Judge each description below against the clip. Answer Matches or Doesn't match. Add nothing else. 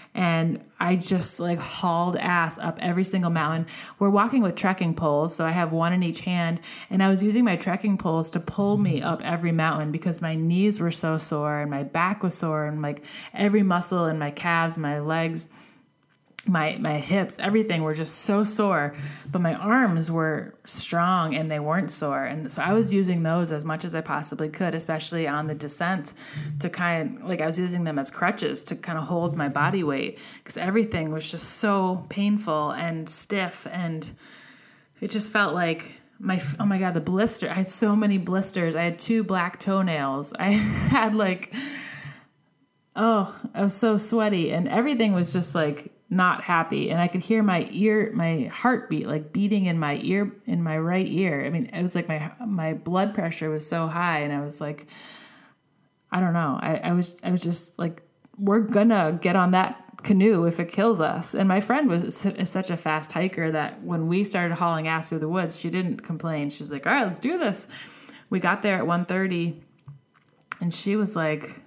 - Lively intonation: Doesn't match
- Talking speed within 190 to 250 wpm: Matches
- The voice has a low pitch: Doesn't match